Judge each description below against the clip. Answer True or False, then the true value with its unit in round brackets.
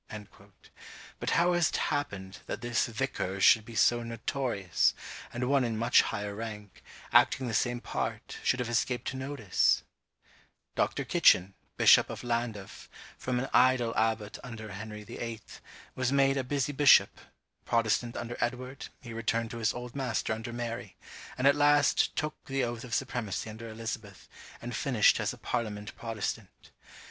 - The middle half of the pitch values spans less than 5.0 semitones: True (2.7 semitones)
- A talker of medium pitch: False (120 Hz)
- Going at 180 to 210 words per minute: False (155 wpm)